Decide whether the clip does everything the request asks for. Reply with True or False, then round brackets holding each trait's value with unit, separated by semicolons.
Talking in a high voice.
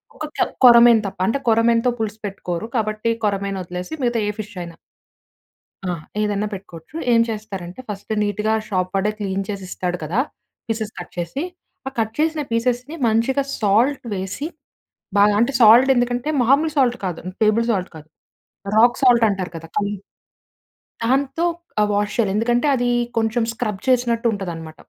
True (220 Hz)